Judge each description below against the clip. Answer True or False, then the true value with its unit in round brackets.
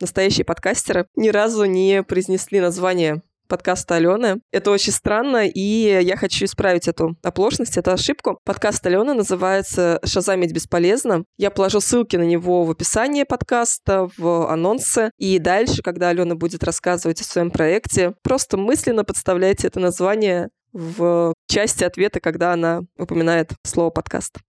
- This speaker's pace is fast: False (140 wpm)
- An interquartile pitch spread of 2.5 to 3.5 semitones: True (2.9 semitones)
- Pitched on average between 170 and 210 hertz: True (185 Hz)